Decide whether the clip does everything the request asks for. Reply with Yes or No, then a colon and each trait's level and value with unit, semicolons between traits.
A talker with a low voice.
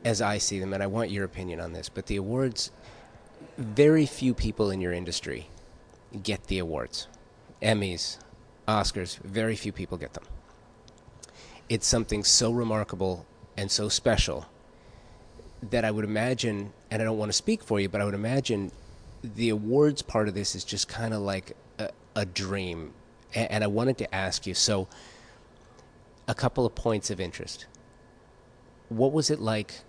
Yes: low, 110 Hz